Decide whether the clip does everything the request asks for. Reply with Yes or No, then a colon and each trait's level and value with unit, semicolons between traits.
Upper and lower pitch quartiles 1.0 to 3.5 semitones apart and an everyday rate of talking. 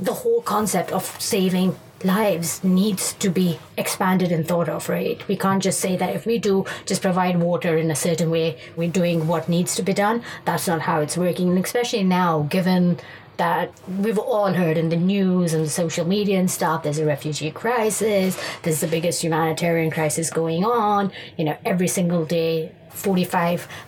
Yes: average, 2.7 semitones; average, 185 wpm